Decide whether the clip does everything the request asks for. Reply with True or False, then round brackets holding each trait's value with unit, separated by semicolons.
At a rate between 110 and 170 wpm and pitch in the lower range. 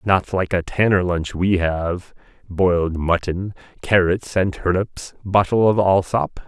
True (140 wpm; 90 Hz)